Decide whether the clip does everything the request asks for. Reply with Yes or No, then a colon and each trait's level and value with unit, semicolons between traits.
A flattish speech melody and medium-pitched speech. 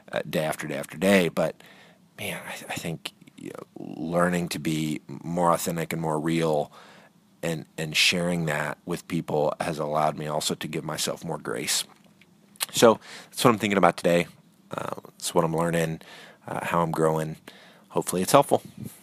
No: narrow, 1.6 semitones; very low, 80 Hz